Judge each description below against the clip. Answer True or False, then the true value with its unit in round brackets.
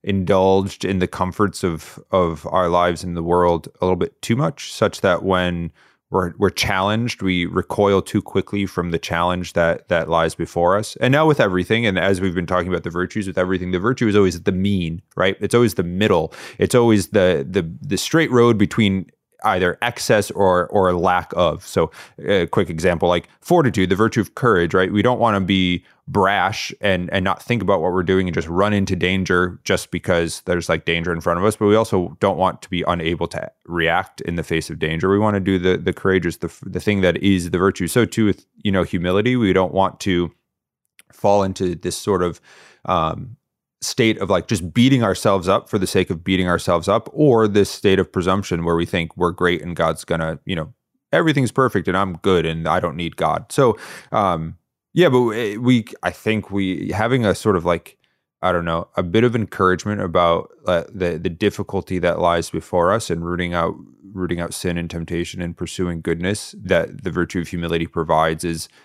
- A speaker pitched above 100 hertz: False (95 Hz)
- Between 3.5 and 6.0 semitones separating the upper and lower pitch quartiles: False (2.7 semitones)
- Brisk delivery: True (215 wpm)